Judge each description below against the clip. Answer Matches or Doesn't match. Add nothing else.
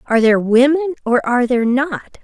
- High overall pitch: Matches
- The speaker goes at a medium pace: Matches